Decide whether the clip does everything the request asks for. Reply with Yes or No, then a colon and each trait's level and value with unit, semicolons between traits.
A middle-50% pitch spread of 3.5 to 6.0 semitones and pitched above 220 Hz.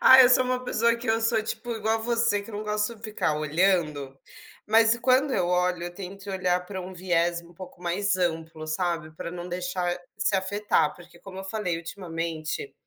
No: average, 4.3 semitones; medium, 185 Hz